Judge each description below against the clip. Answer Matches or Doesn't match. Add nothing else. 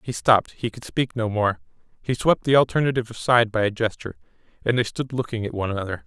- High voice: Doesn't match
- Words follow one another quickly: Matches